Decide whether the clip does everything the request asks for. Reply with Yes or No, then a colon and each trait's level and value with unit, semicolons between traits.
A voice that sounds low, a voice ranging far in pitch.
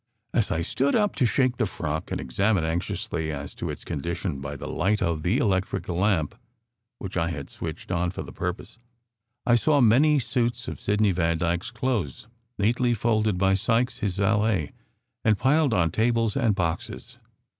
Yes: low, 100 Hz; wide, 5.7 semitones